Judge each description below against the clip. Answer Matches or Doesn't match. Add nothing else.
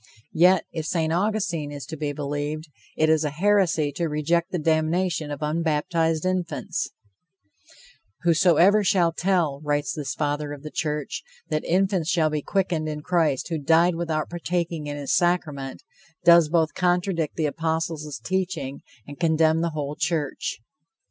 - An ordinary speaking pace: Matches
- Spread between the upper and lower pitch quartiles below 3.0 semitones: Matches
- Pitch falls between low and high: Matches